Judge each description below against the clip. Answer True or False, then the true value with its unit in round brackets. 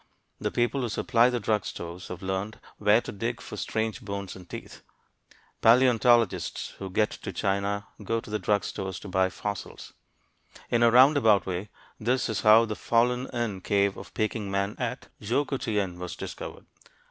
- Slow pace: False (170 wpm)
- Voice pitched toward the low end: True (105 Hz)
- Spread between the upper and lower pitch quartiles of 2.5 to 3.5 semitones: True (3.2 semitones)